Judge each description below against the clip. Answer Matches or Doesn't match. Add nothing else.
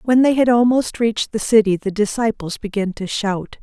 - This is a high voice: Matches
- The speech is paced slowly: Doesn't match